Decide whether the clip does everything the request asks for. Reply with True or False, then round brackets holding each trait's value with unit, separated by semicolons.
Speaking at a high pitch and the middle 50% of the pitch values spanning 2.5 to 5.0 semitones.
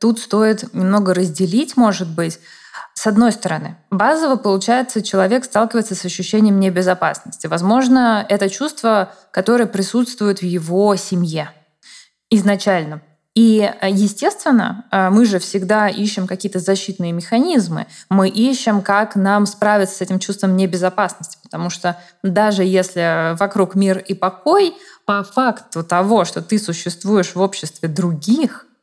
True (200 Hz; 3.4 semitones)